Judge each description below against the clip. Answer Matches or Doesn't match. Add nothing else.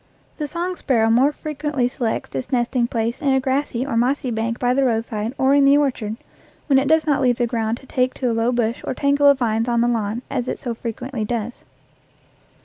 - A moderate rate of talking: Doesn't match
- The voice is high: Matches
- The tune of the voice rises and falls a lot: Doesn't match